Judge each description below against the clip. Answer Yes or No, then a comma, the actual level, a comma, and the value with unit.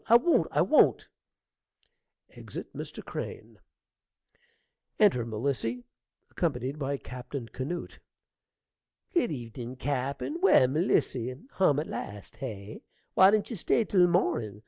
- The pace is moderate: No, slow, 115 wpm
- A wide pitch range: Yes, wide, 6.6 semitones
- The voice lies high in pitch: No, low, 135 Hz